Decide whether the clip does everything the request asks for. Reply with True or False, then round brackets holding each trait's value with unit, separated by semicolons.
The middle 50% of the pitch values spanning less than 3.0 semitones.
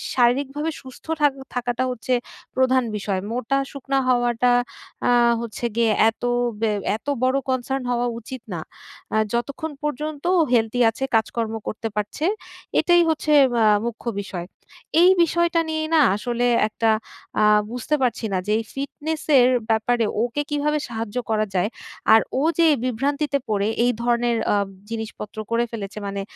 False (3.8 semitones)